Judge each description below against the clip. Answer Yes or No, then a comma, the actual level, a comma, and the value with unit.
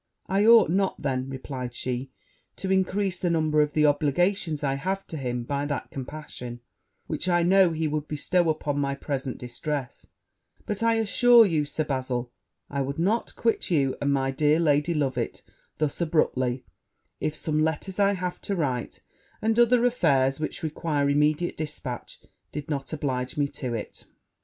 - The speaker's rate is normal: Yes, average, 165 wpm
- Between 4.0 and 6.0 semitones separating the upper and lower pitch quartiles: Yes, average, 4.5 semitones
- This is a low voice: No, medium, 150 Hz